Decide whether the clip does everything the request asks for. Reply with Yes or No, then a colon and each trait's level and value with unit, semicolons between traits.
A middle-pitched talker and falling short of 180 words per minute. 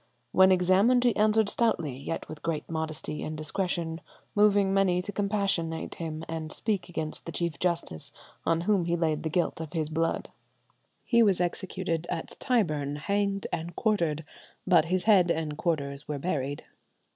Yes: medium, 170 Hz; average, 160 wpm